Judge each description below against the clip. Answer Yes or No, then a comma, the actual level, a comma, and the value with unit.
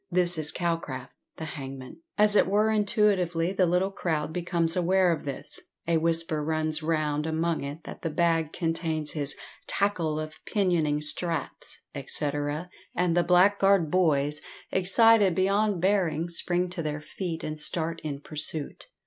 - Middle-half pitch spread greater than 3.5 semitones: No, average, 3.0 semitones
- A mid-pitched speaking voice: Yes, medium, 165 Hz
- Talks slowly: No, average, 150 wpm